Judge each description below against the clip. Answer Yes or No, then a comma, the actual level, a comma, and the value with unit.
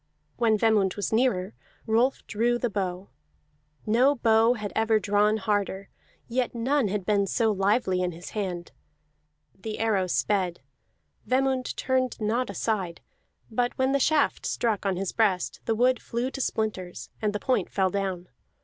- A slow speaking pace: No, average, 155 wpm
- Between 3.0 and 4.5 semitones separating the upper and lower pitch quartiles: Yes, average, 3.8 semitones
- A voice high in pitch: Yes, high, 215 Hz